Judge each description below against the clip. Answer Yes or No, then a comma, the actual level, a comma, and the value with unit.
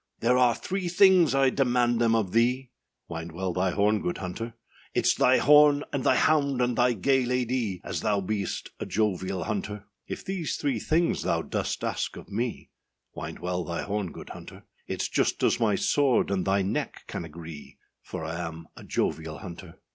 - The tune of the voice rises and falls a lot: Yes, wide, 5.9 semitones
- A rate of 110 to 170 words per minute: No, average, 185 wpm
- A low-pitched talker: Yes, low, 110 Hz